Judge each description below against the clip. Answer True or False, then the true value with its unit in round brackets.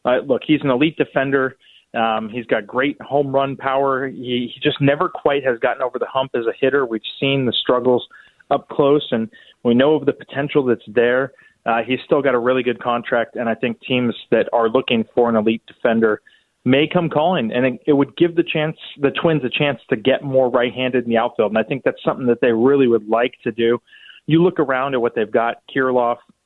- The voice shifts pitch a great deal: False (2.9 semitones)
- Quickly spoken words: True (225 wpm)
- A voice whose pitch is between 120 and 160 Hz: True (130 Hz)